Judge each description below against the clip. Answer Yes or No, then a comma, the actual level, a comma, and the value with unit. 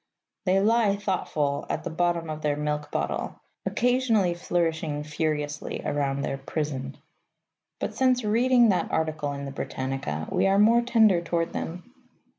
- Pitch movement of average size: No, wide, 6.0 semitones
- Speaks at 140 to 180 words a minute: Yes, average, 145 wpm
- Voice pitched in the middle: Yes, medium, 165 Hz